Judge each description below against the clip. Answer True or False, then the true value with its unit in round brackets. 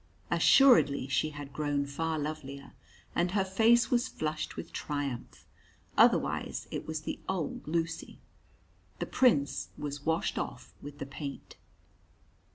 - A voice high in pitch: False (155 Hz)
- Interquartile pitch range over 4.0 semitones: False (3.3 semitones)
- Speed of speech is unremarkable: False (130 wpm)